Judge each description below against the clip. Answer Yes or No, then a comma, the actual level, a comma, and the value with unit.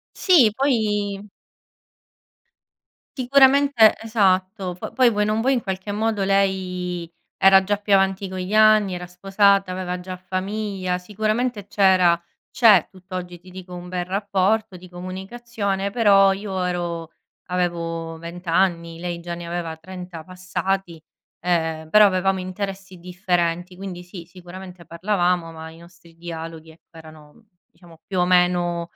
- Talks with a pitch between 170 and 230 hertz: Yes, medium, 185 Hz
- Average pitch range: No, narrow, 2.3 semitones